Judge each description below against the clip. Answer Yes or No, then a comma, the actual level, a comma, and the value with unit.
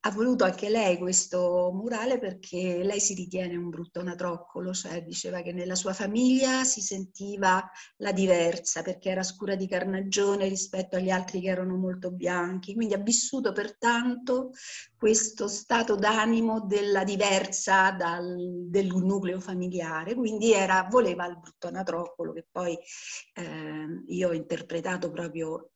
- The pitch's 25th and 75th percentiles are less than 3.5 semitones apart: Yes, narrow, 2.6 semitones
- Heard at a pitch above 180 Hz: Yes, high, 190 Hz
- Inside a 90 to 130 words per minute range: No, average, 140 wpm